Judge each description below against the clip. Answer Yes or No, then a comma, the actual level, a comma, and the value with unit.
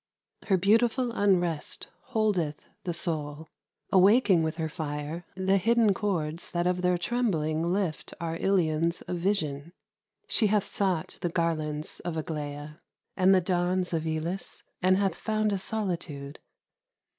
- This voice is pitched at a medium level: Yes, medium, 175 Hz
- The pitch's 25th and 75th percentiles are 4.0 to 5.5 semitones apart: No, average, 3.6 semitones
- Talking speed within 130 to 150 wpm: Yes, slow, 135 wpm